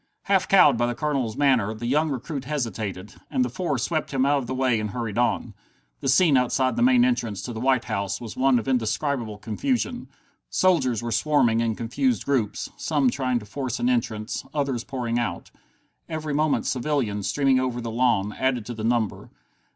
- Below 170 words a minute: No, average, 190 wpm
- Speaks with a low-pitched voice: Yes, low, 125 Hz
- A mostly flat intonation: No, average, 4.2 semitones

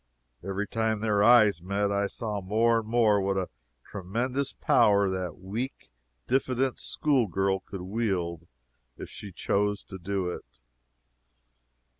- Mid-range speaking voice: No, low, 100 Hz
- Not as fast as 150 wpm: Yes, slow, 135 wpm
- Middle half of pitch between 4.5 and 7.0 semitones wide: No, average, 2.9 semitones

